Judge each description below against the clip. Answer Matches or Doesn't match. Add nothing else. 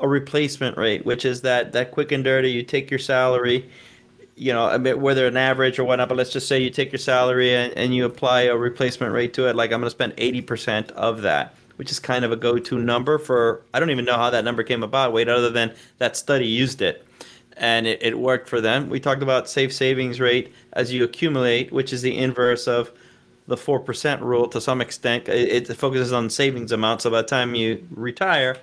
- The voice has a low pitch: Matches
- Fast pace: Matches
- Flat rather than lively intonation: Matches